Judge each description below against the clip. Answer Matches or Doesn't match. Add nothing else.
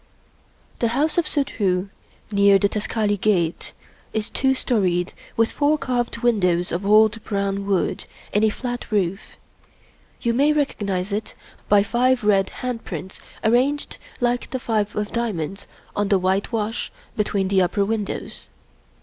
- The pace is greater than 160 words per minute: Doesn't match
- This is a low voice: Doesn't match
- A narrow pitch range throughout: Doesn't match